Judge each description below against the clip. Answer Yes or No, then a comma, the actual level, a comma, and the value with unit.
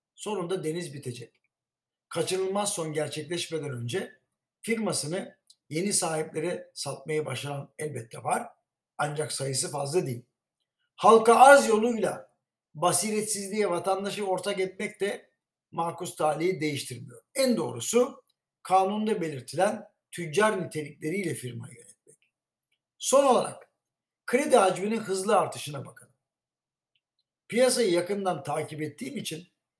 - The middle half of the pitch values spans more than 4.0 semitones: Yes, average, 5.3 semitones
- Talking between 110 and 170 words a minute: No, average, 100 wpm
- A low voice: No, medium, 180 Hz